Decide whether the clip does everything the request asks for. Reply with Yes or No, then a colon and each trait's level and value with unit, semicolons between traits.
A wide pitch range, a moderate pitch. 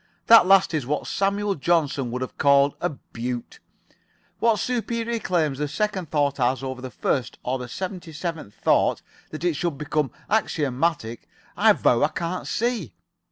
Yes: wide, 6.2 semitones; medium, 155 Hz